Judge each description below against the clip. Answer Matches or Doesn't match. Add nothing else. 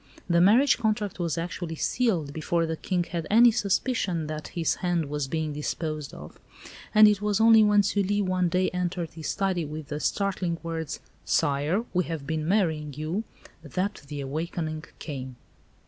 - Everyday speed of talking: Matches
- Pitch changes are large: Doesn't match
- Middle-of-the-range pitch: Matches